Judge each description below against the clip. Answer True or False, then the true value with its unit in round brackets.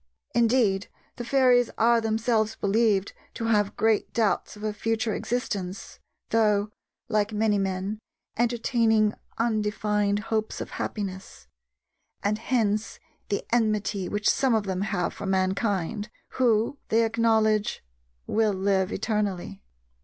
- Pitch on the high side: True (215 Hz)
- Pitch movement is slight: True (2.0 semitones)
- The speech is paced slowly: True (120 wpm)